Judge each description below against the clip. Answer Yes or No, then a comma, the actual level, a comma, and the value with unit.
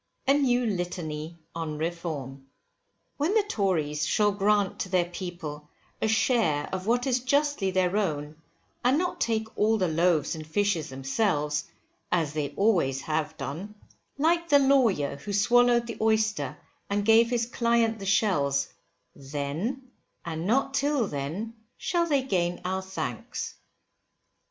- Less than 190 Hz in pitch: No, high, 195 Hz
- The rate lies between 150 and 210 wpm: No, average, 140 wpm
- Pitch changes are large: Yes, wide, 7.0 semitones